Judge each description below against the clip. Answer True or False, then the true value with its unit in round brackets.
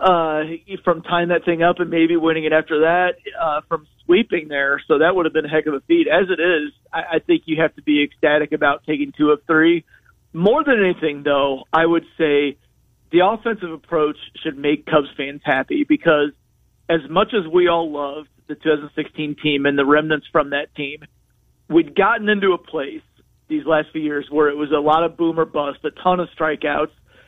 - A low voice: False (155 Hz)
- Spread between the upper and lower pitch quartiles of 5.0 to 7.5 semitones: False (2.7 semitones)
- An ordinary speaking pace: False (210 wpm)